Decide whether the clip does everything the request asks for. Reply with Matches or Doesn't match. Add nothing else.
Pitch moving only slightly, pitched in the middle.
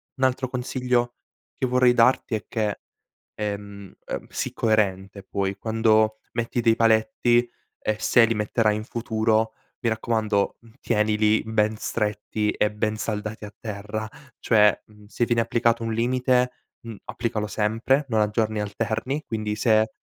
Doesn't match